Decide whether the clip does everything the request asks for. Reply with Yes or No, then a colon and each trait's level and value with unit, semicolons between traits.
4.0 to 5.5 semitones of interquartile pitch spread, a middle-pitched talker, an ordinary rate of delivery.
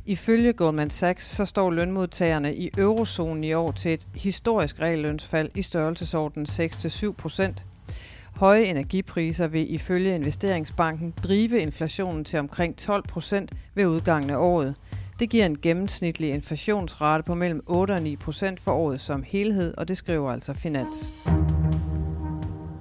No: average, 4.4 semitones; medium, 165 Hz; slow, 135 wpm